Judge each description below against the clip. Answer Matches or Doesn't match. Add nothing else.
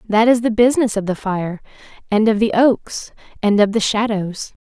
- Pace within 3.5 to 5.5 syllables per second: Matches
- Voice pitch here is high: Matches